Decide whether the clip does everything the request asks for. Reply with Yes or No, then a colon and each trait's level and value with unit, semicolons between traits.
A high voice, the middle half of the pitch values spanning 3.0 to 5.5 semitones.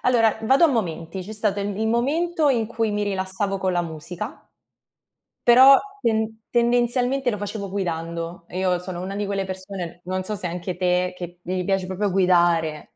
Yes: high, 195 Hz; average, 3.8 semitones